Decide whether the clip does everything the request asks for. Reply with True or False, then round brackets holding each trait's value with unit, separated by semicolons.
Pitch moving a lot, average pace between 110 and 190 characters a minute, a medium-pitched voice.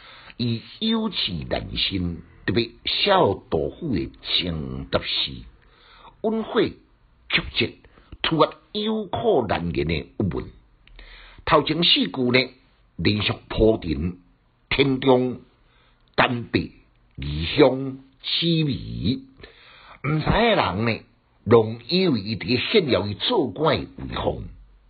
False (7.0 semitones; 145 characters per minute; 125 Hz)